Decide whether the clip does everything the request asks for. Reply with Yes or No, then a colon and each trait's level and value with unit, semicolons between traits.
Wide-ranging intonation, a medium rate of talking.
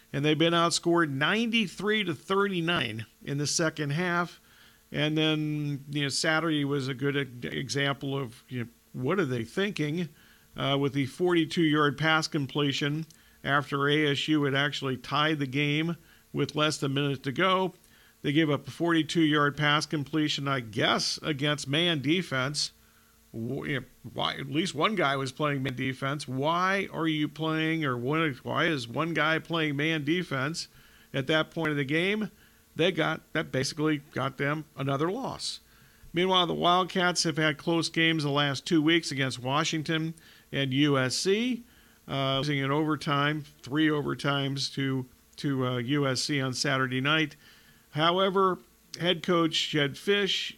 No: average, 2.9 semitones; average, 160 wpm